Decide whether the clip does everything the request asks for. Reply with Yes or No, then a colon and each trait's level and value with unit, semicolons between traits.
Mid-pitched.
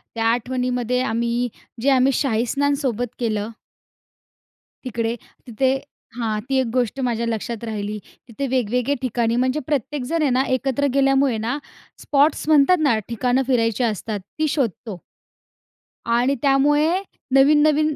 No: very high, 250 Hz